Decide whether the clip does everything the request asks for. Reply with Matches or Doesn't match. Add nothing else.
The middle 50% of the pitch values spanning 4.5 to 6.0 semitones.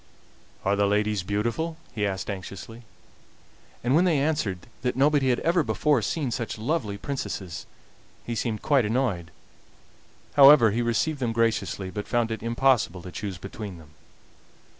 Matches